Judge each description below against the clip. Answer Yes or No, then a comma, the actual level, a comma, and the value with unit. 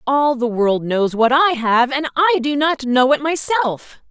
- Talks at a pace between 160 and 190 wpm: No, fast, 205 wpm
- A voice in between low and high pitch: No, very high, 270 Hz